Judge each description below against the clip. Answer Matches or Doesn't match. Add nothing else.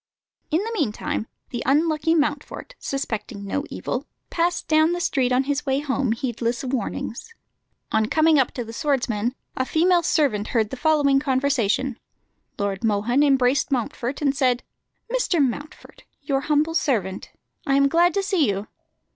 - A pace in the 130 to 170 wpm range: Matches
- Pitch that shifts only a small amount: Doesn't match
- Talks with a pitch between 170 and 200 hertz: Doesn't match